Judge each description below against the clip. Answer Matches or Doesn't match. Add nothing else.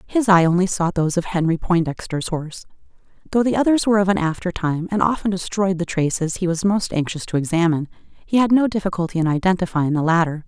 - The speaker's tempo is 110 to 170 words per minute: Doesn't match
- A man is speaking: Doesn't match